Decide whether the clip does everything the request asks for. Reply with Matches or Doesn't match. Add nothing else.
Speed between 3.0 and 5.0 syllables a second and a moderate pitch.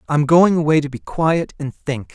Matches